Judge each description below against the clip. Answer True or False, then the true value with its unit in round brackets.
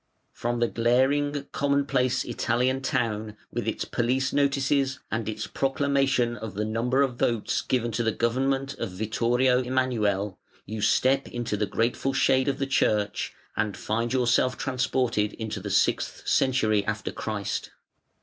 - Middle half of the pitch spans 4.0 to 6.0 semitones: False (3.3 semitones)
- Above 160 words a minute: False (145 wpm)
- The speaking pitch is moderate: False (120 Hz)